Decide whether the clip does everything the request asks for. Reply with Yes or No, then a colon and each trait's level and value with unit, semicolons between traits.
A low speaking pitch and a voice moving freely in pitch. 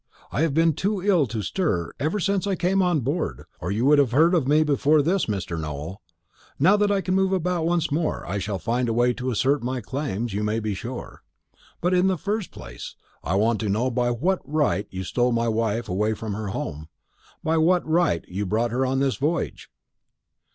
Yes: low, 130 Hz; wide, 7.8 semitones